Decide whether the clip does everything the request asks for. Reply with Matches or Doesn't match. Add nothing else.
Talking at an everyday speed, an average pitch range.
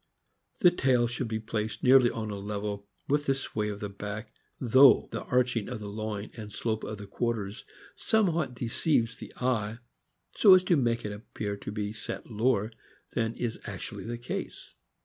Matches